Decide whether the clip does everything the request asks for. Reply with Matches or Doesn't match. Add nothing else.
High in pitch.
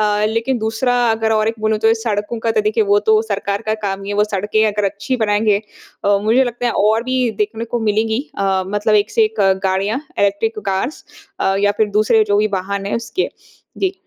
Matches